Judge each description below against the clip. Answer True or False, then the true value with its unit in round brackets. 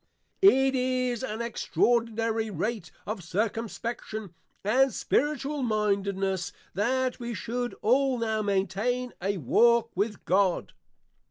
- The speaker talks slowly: True (110 wpm)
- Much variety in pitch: False (3.6 semitones)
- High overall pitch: True (230 Hz)